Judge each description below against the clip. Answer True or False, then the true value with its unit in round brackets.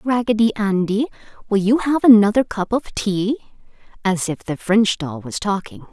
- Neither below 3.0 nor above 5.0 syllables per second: True (4.8 syllables/s)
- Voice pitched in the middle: False (210 Hz)